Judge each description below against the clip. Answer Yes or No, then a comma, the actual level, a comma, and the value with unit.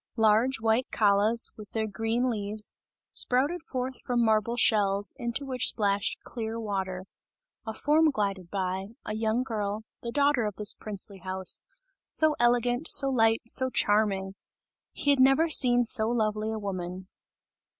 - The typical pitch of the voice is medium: No, high, 220 Hz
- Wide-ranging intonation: No, average, 3.4 semitones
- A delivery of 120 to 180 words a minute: Yes, average, 150 wpm